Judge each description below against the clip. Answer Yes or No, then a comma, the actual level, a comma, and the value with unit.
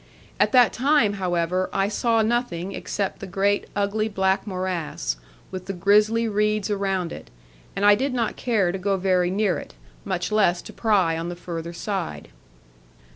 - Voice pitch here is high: Yes, high, 195 Hz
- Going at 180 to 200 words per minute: No, average, 170 wpm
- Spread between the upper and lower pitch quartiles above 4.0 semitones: No, average, 2.8 semitones